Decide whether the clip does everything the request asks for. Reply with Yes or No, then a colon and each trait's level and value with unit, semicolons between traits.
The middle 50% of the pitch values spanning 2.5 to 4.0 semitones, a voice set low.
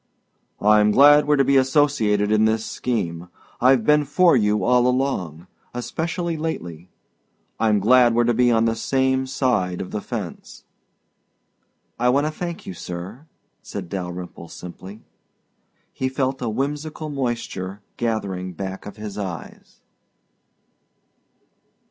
No: average, 5.2 semitones; low, 115 Hz